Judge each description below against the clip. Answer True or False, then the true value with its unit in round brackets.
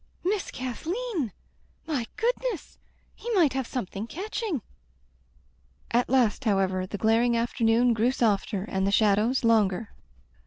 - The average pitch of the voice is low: False (235 Hz)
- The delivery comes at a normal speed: False (120 wpm)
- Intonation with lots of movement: True (5.9 semitones)